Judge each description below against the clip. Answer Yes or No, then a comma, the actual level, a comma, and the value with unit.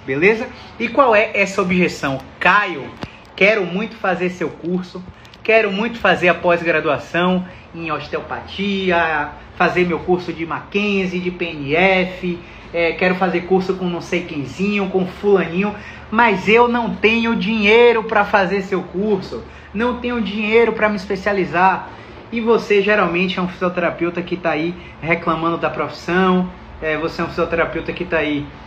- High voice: No, medium, 180 Hz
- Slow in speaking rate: No, average, 150 wpm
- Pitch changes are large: No, average, 3.4 semitones